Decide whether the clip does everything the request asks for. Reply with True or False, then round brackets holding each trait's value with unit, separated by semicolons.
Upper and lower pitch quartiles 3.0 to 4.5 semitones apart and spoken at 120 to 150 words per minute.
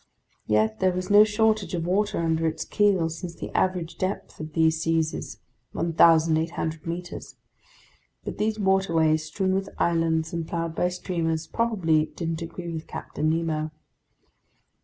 False (2.6 semitones; 145 wpm)